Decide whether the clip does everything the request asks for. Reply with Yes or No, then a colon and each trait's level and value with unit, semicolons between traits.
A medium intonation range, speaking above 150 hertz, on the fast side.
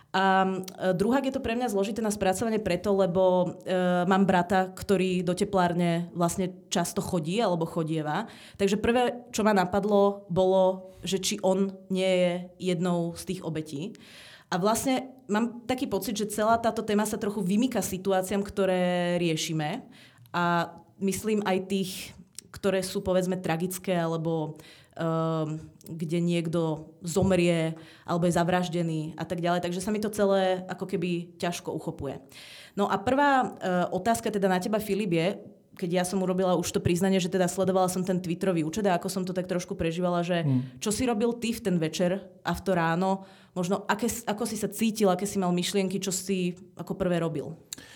No: narrow, 2.3 semitones; medium, 185 Hz; fast, 175 wpm